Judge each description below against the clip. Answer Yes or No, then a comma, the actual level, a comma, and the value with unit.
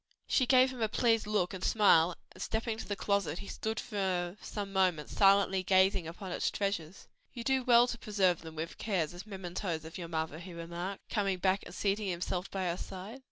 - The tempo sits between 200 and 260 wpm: Yes, fast, 205 wpm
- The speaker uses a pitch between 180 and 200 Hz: Yes, high, 190 Hz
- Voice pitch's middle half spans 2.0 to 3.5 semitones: Yes, average, 3.1 semitones